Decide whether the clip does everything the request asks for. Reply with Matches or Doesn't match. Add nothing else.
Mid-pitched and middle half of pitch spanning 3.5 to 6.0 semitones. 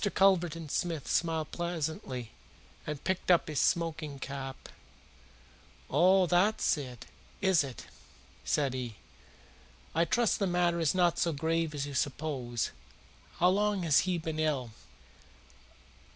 Matches